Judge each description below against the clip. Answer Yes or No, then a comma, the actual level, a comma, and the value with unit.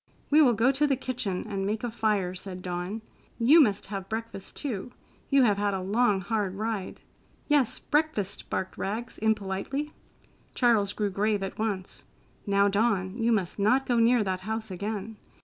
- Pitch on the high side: Yes, high, 215 Hz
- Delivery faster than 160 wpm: Yes, average, 170 wpm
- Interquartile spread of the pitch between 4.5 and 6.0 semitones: No, average, 3.4 semitones